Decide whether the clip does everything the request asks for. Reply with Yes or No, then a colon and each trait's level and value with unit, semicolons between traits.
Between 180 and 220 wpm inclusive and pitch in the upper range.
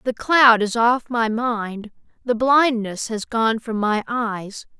No: average, 165 wpm; high, 230 Hz